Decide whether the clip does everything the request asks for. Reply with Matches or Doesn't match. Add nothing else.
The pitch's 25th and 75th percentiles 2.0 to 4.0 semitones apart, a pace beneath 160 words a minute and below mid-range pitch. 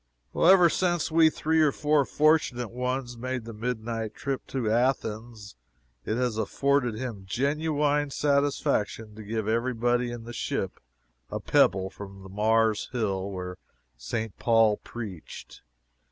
Doesn't match